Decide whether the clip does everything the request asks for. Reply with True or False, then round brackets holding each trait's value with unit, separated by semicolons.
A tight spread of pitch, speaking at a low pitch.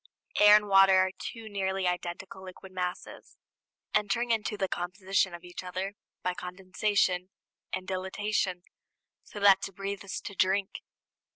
False (1.7 semitones; 190 Hz)